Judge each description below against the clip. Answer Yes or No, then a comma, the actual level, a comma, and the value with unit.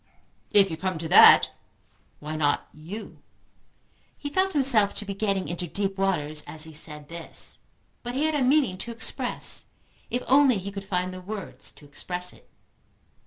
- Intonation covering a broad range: Yes, wide, 6.1 semitones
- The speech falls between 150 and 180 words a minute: Yes, average, 170 wpm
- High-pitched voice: Yes, high, 195 Hz